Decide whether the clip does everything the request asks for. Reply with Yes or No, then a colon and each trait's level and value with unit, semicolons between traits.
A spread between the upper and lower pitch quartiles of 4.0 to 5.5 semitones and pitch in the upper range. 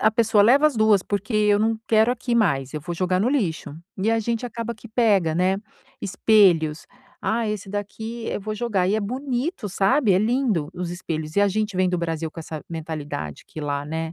Yes: average, 5.1 semitones; high, 205 Hz